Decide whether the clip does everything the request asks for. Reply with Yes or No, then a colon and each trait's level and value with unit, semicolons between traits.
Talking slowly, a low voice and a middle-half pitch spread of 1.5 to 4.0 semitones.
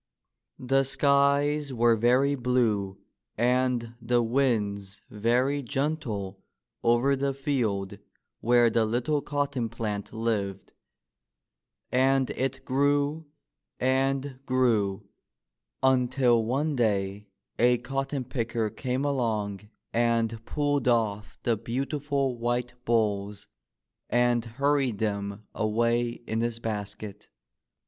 Yes: slow, 100 wpm; low, 120 Hz; average, 3.6 semitones